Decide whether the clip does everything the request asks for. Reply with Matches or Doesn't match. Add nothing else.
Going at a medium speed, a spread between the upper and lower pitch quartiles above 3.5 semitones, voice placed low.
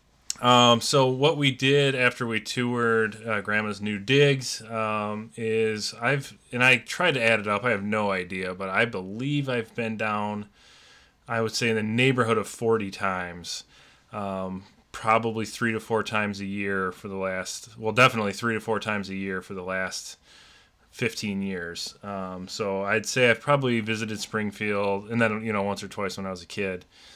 Doesn't match